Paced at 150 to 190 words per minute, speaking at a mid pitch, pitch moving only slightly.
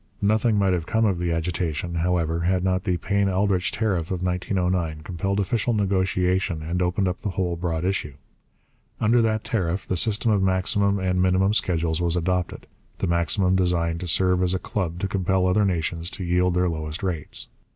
No: average, 185 wpm; very low, 90 Hz; narrow, 2.2 semitones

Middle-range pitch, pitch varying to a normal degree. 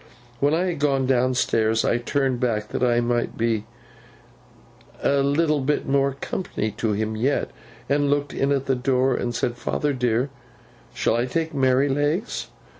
No: low, 130 Hz; average, 3.1 semitones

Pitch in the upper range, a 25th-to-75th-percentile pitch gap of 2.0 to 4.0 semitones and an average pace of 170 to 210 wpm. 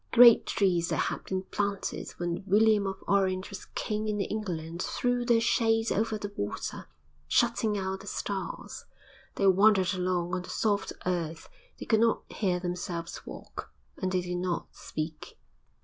No: high, 195 Hz; average, 3.2 semitones; average, 160 wpm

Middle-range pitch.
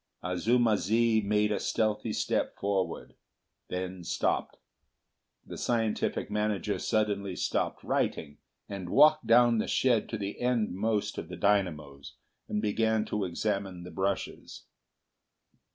No: low, 105 Hz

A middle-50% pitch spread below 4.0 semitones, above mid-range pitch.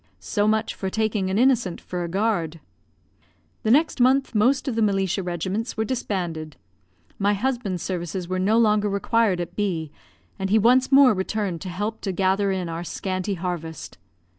Yes: average, 3.5 semitones; high, 200 Hz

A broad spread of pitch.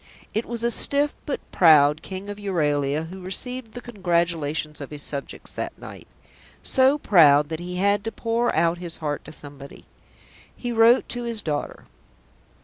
Yes: wide, 7.2 semitones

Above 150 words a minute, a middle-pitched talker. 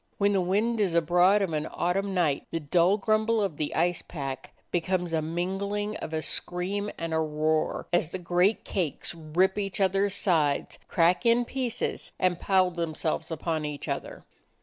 Yes: average, 175 wpm; medium, 180 Hz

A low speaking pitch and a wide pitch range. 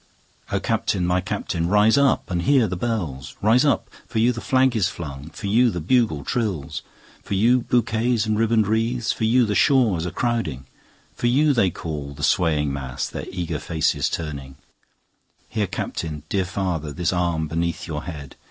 Yes: very low, 95 Hz; wide, 6.4 semitones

